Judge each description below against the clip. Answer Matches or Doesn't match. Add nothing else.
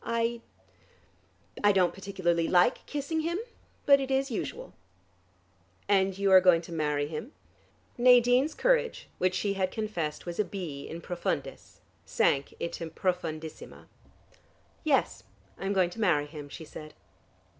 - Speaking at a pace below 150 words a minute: Matches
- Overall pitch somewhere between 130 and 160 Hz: Doesn't match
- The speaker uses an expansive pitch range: Matches